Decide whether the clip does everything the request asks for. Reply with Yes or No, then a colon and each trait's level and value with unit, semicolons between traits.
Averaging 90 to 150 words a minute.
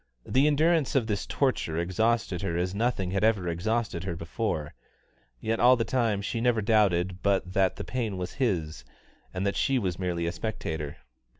No: average, 180 wpm